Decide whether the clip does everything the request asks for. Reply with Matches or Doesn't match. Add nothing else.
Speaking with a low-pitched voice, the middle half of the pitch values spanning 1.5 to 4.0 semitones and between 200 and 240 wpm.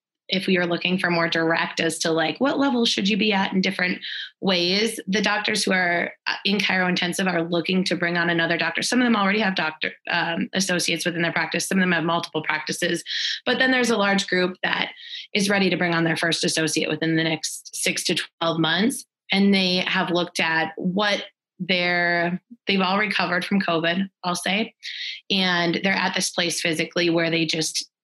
Doesn't match